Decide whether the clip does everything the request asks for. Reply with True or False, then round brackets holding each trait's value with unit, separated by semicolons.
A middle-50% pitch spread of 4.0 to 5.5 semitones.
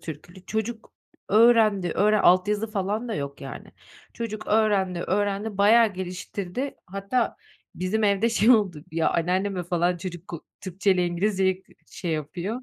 False (3.2 semitones)